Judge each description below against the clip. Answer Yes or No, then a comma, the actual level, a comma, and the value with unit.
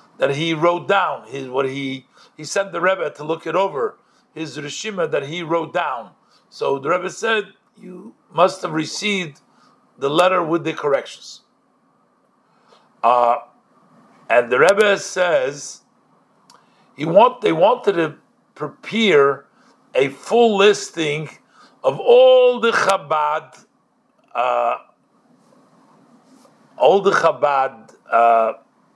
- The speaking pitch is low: No, high, 190 Hz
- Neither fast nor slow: No, slow, 120 wpm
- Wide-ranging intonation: Yes, wide, 6.9 semitones